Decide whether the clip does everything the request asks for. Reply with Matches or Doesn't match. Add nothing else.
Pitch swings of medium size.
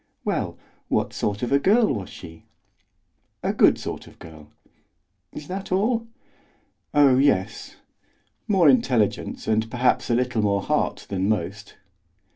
Doesn't match